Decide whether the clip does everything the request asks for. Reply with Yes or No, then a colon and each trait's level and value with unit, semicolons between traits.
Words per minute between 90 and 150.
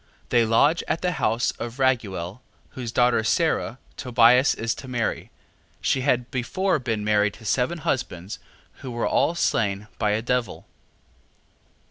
Yes: average, 145 wpm